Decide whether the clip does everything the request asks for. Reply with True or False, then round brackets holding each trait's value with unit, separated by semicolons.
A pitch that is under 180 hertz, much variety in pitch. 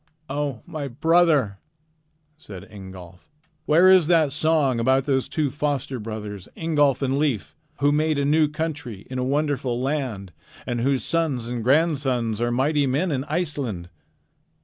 False (140 Hz; 4.1 semitones)